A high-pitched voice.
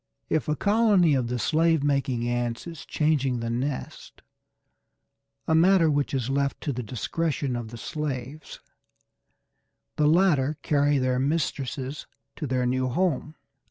No: medium, 140 Hz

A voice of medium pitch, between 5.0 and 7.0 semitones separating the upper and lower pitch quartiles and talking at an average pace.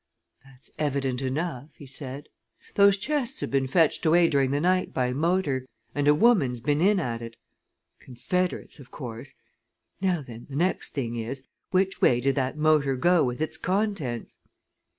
Yes: medium, 145 Hz; wide, 5.4 semitones; average, 165 wpm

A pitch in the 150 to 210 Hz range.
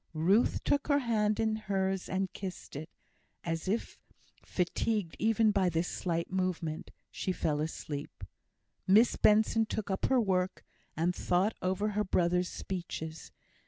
Yes: high, 190 Hz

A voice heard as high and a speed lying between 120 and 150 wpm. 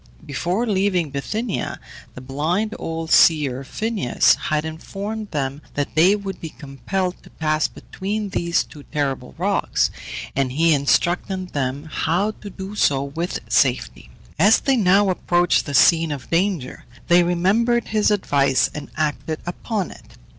No: medium, 170 Hz; average, 140 wpm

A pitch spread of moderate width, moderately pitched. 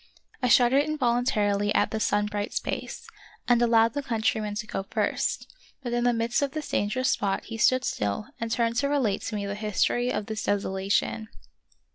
No: average, 3.1 semitones; high, 225 Hz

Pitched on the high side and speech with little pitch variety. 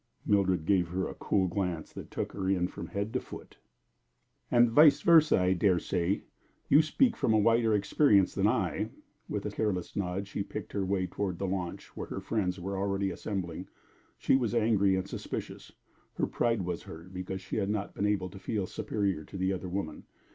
No: very low, 95 Hz; narrow, 2.2 semitones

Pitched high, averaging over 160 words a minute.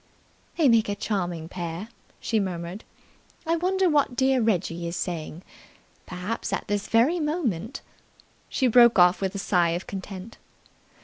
No: high, 205 Hz; average, 150 wpm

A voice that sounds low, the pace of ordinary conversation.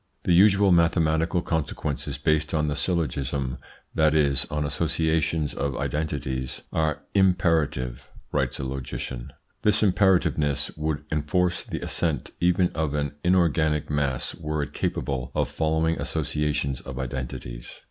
No: very low, 75 Hz; slow, 130 wpm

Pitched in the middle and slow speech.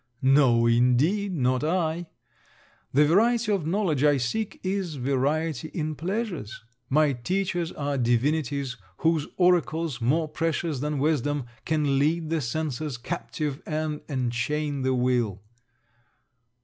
Yes: medium, 150 Hz; slow, 120 wpm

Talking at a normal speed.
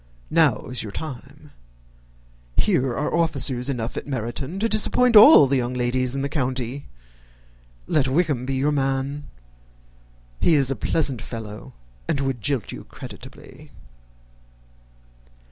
No: slow, 130 wpm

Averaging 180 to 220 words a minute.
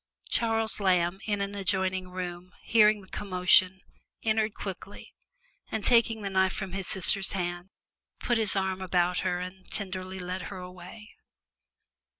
No: average, 145 wpm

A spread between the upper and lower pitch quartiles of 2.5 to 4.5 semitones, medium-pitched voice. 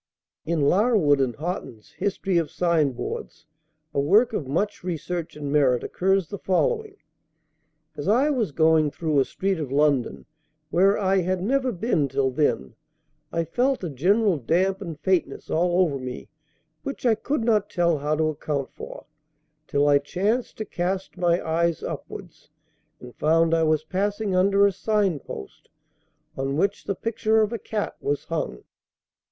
No: average, 5.3 semitones; medium, 175 Hz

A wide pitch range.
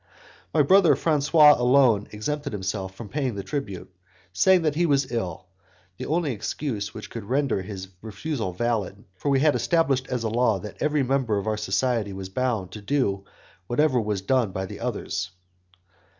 Yes: wide, 5.9 semitones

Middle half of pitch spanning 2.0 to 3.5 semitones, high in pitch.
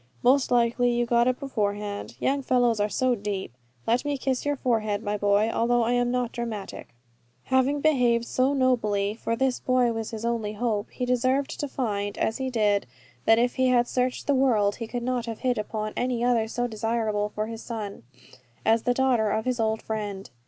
Yes: average, 2.8 semitones; high, 235 Hz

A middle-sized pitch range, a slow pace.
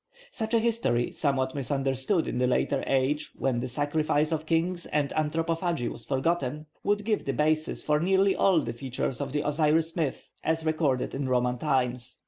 No: average, 3.8 semitones; average, 175 wpm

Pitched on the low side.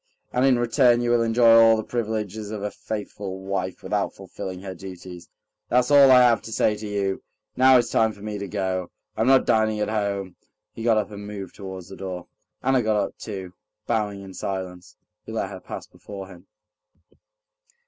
Yes: low, 105 Hz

